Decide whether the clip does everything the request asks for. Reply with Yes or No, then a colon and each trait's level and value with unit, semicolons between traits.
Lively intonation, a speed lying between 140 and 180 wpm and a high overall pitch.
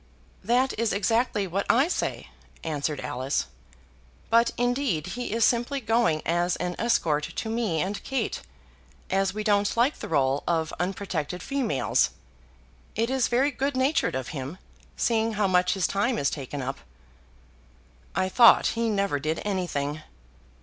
Yes: wide, 6.6 semitones; average, 150 wpm; high, 200 Hz